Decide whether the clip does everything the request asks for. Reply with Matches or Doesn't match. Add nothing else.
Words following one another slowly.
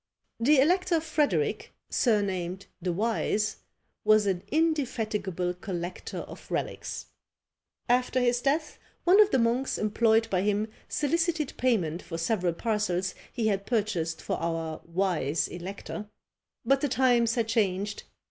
Matches